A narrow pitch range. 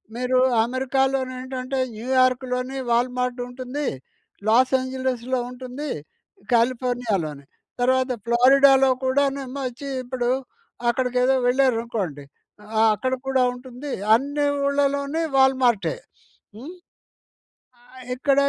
Yes: narrow, 1.4 semitones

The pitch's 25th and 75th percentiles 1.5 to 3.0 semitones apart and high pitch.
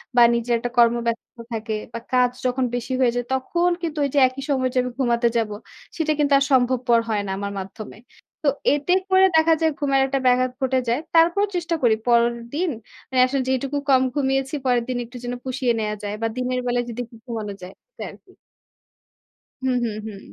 Yes: average, 2.7 semitones; very high, 255 Hz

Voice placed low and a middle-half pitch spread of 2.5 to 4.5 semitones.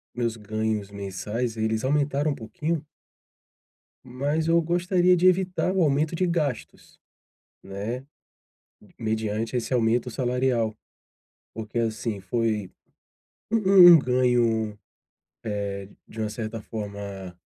No: low, 115 Hz; wide, 5.4 semitones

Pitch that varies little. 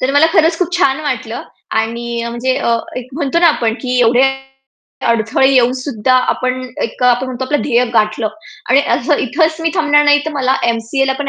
No: average, 3.5 semitones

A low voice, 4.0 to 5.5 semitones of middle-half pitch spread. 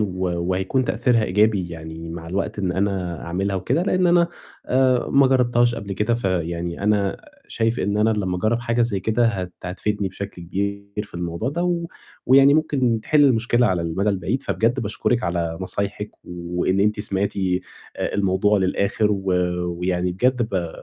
Yes: low, 100 Hz; average, 4.4 semitones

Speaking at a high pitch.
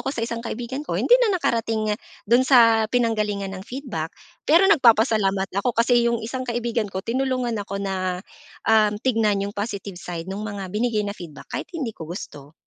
Yes: high, 220 Hz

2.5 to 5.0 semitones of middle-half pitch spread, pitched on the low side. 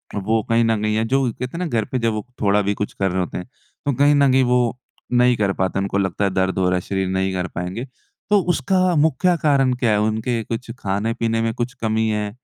Yes: average, 4.3 semitones; low, 110 Hz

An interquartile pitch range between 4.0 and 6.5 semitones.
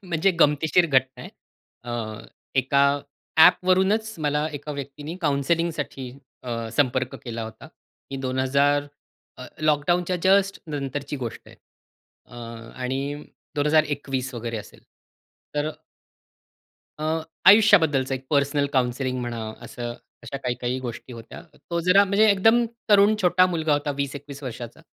Yes: average, 4.6 semitones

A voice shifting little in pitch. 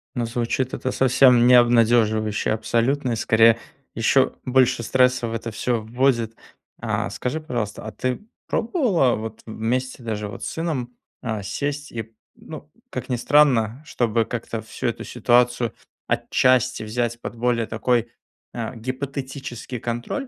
Yes: narrow, 2.3 semitones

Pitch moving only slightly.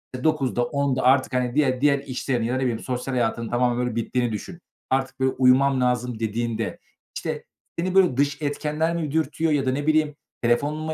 No: average, 3.1 semitones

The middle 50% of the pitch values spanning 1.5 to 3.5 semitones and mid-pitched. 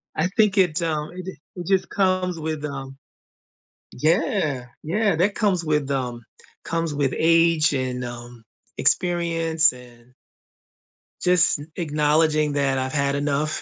No: average, 3.9 semitones; medium, 155 Hz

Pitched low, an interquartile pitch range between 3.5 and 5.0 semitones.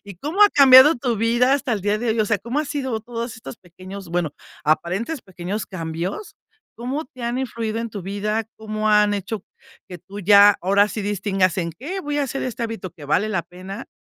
No: high, 215 Hz; average, 4.2 semitones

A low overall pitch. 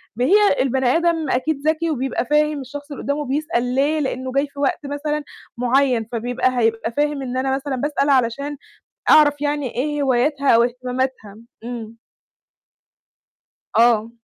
No: very high, 270 Hz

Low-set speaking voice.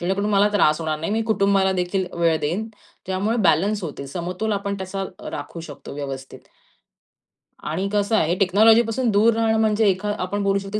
No: high, 195 Hz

